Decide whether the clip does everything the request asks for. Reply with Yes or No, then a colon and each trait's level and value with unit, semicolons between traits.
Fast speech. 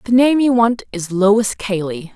No: average, 165 wpm